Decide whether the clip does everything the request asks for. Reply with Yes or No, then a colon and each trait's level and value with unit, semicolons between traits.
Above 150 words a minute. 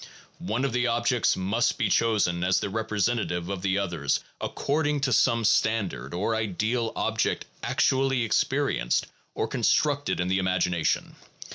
No: average, 140 wpm